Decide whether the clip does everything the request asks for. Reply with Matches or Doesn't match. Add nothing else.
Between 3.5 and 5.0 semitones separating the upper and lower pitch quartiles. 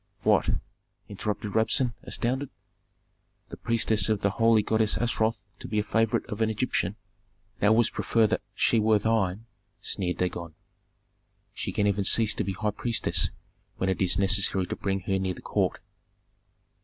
Doesn't match